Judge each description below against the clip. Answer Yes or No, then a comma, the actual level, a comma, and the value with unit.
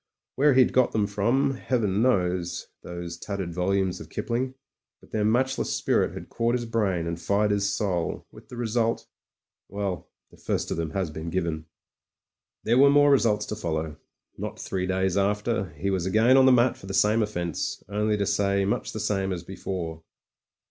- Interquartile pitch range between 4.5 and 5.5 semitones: No, average, 4.0 semitones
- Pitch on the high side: No, low, 100 Hz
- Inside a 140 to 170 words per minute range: No, average, 185 wpm